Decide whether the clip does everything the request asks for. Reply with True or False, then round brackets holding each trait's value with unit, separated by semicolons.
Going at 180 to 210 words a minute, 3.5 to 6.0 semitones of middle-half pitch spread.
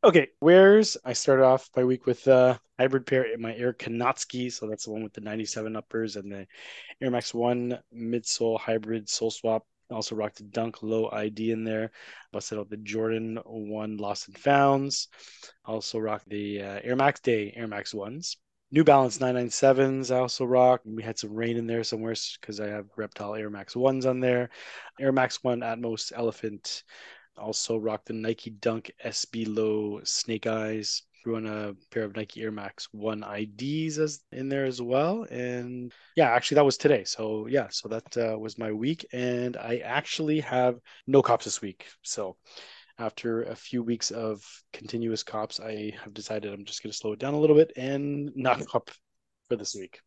False (190 wpm; 2.8 semitones)